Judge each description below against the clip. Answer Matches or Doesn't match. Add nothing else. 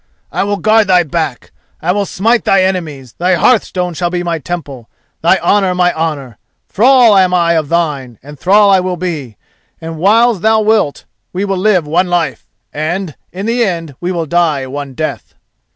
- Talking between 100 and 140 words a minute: Doesn't match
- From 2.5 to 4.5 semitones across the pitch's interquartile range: Matches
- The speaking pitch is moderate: Matches